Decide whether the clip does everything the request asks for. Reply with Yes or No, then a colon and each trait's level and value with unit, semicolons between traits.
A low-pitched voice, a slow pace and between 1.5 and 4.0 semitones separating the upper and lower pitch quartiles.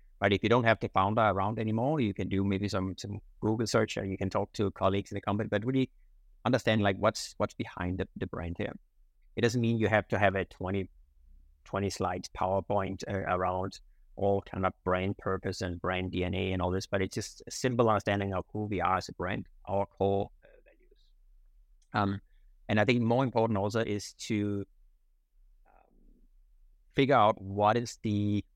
No: low, 100 Hz; average, 195 wpm; narrow, 2.5 semitones